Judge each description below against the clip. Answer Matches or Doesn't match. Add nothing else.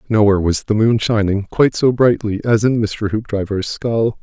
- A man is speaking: Matches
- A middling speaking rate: Matches